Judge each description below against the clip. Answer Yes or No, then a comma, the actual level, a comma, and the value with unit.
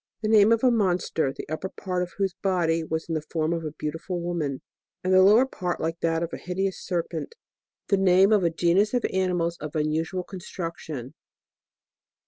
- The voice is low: No, medium, 175 Hz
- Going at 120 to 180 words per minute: No, average, 195 wpm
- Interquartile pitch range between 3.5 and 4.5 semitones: No, average, 2.7 semitones